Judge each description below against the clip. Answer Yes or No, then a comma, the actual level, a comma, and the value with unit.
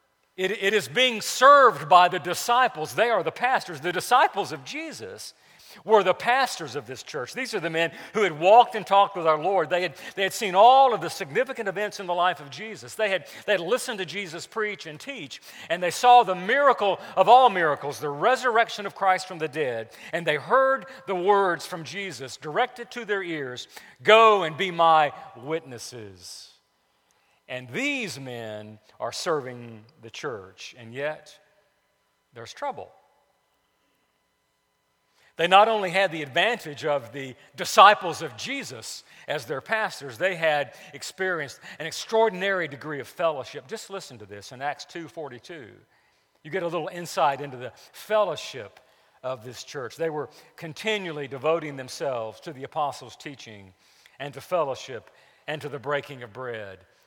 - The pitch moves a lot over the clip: Yes, wide, 6.4 semitones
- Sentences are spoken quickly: No, average, 165 wpm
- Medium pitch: Yes, medium, 170 Hz